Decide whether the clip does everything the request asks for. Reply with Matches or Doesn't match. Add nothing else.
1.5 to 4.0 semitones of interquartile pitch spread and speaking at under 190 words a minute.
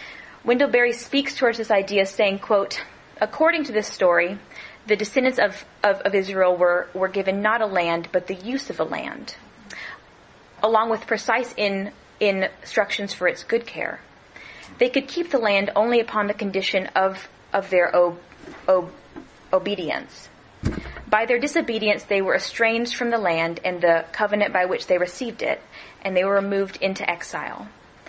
Matches